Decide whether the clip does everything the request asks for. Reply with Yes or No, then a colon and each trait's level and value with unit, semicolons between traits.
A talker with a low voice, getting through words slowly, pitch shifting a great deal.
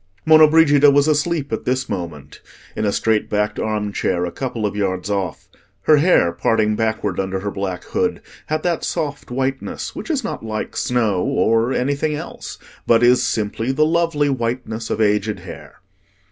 No: low, 115 Hz; average, 175 wpm; wide, 5.7 semitones